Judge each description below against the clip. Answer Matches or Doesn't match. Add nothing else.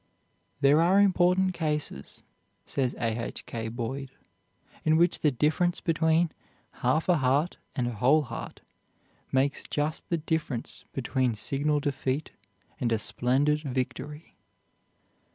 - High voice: Doesn't match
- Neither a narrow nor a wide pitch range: Matches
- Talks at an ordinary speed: Doesn't match